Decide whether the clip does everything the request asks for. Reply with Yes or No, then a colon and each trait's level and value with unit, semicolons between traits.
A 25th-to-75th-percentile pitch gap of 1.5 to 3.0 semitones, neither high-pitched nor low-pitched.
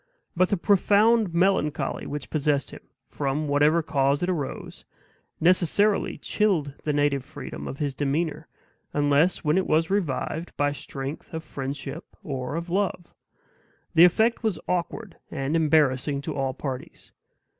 No: average, 4.0 semitones; medium, 155 Hz